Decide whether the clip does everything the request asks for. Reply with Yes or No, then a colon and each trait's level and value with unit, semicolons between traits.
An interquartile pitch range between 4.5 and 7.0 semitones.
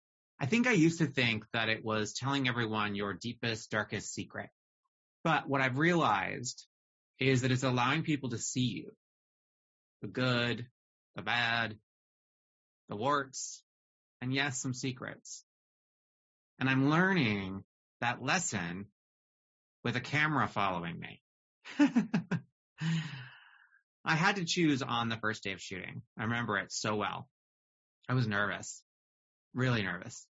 Yes: average, 4.8 semitones